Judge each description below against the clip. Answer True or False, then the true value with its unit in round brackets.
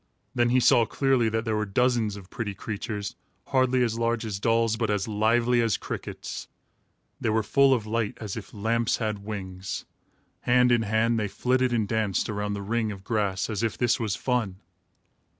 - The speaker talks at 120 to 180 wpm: False (190 wpm)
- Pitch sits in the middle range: False (110 Hz)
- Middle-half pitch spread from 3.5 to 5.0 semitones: False (2.5 semitones)